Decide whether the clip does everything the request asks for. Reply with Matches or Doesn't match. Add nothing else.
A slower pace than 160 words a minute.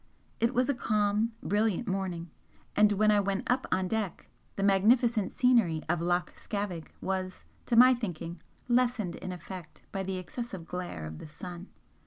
Doesn't match